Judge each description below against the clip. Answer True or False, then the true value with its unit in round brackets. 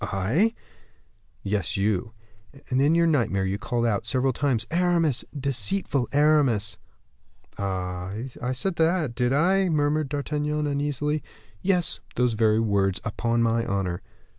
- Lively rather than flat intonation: True (5.9 semitones)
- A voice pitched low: True (130 Hz)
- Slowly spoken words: True (130 wpm)